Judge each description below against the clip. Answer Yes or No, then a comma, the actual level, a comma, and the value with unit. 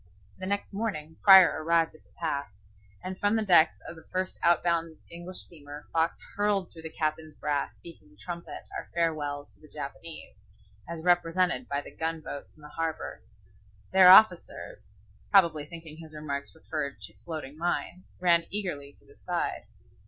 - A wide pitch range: No, average, 2.8 semitones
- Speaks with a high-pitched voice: No, medium, 165 Hz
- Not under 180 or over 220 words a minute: No, average, 165 wpm